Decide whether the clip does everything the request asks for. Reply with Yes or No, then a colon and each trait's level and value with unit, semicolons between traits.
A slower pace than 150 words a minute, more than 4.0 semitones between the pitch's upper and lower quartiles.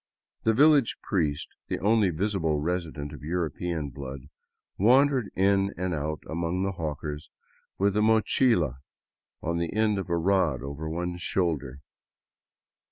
Yes: slow, 135 wpm; average, 4.5 semitones